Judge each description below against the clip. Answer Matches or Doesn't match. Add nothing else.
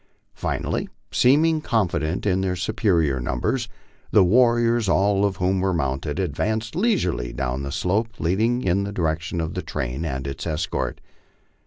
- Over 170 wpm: Doesn't match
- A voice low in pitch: Matches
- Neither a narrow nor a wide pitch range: Doesn't match